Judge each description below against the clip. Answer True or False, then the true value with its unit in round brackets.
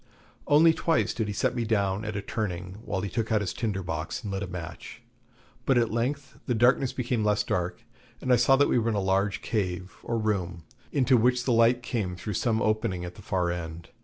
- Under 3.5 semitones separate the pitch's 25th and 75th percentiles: False (4.3 semitones)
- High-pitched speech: False (105 Hz)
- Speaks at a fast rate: True (225 wpm)